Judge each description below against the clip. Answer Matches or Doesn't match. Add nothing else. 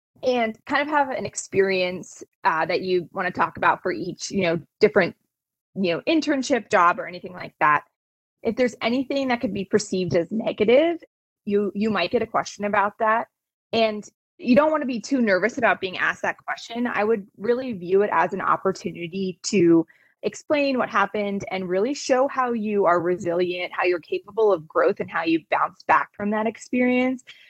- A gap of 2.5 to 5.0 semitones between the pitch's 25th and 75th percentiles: Doesn't match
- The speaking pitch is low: Doesn't match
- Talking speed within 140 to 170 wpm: Doesn't match